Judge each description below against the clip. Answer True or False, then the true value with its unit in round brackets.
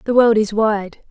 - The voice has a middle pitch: False (215 Hz)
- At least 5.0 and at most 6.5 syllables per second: False (4.4 syllables/s)